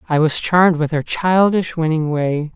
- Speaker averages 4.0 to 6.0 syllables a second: Yes, 4.6 syllables/s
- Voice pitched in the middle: Yes, medium, 165 Hz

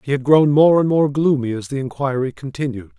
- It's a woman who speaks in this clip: No, male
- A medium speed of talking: No, fast, 220 wpm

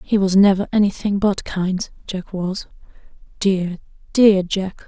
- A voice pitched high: Yes, high, 195 Hz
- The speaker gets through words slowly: Yes, slow, 110 wpm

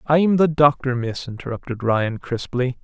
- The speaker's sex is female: No, male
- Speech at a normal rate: Yes, average, 150 wpm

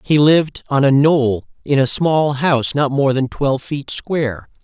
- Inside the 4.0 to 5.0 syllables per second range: Yes, 4.5 syllables/s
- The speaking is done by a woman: No, male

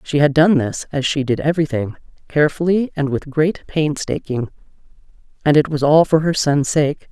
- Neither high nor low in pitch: Yes, medium, 150 Hz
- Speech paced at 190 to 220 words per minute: No, average, 175 wpm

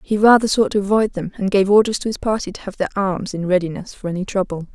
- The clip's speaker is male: No, female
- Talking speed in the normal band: No, fast, 265 wpm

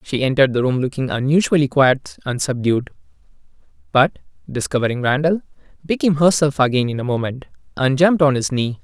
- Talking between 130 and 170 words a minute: Yes, average, 150 wpm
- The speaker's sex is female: No, male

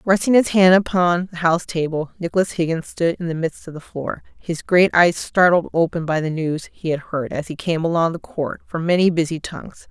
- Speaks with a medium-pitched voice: Yes, medium, 170 Hz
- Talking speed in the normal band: No, fast, 225 wpm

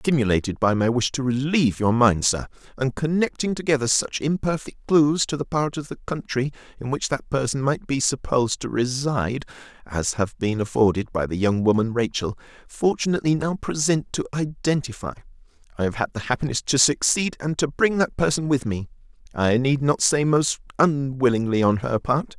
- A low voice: Yes, low, 130 Hz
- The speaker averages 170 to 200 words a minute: Yes, average, 175 wpm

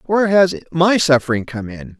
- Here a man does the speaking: Yes, male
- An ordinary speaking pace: Yes, average, 180 wpm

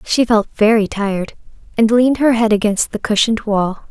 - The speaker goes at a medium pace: Yes, average, 185 wpm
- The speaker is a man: No, female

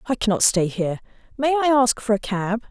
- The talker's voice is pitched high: Yes, high, 230 Hz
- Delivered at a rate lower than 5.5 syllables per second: No, 5.6 syllables/s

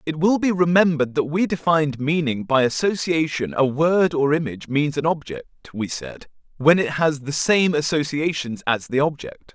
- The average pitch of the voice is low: No, medium, 150 Hz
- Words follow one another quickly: No, average, 175 wpm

